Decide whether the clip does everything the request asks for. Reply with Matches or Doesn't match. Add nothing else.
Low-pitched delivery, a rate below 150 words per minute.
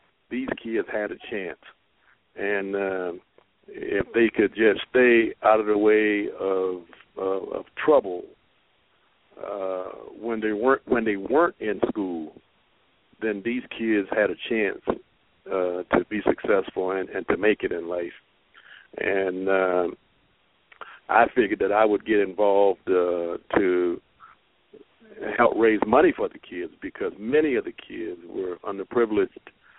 Matches